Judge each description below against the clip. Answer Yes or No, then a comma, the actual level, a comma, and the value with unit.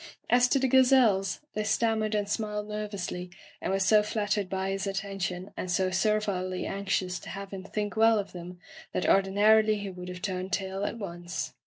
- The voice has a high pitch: Yes, high, 200 Hz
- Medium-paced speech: Yes, average, 185 wpm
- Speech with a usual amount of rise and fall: No, narrow, 2.2 semitones